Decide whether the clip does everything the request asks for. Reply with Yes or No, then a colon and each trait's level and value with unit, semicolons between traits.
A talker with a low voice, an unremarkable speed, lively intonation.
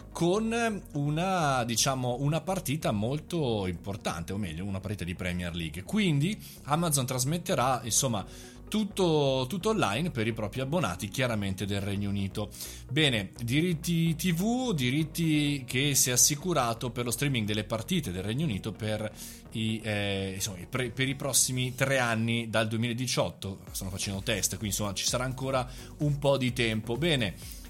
Yes: low, 125 Hz; average, 155 wpm; wide, 6.0 semitones